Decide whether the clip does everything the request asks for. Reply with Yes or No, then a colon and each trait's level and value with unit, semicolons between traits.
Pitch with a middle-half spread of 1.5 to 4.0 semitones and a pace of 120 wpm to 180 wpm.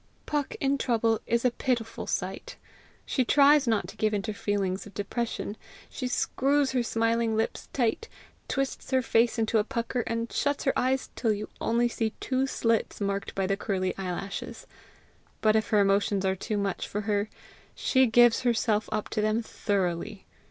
Yes: average, 3.4 semitones; average, 175 wpm